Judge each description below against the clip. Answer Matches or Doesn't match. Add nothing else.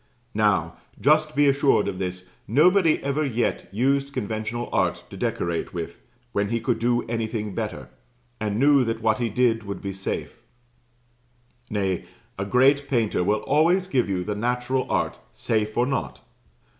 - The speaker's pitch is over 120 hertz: Doesn't match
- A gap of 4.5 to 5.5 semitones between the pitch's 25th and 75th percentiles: Matches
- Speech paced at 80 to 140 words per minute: Doesn't match